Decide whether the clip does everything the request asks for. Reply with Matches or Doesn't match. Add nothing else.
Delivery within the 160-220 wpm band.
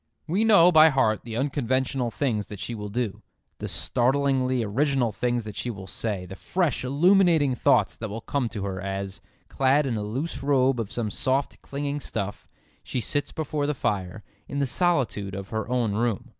Matches